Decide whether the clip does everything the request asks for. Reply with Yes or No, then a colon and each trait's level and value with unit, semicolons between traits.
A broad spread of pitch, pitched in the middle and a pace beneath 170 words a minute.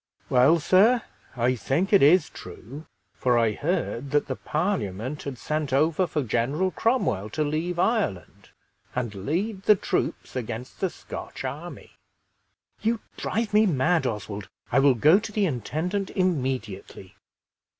Yes: wide, 7.1 semitones; medium, 150 Hz; average, 140 wpm